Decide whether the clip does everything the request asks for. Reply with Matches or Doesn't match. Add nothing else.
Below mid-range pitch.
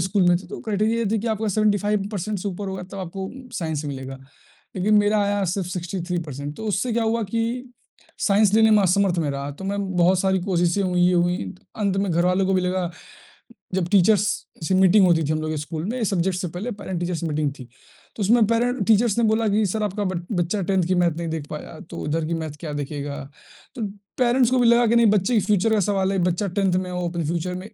Doesn't match